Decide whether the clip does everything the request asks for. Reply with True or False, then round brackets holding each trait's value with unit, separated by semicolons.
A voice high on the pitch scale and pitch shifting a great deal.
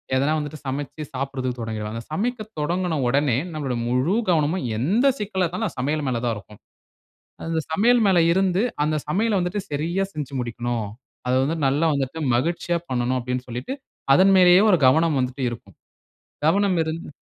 False (150 Hz; 6.0 semitones)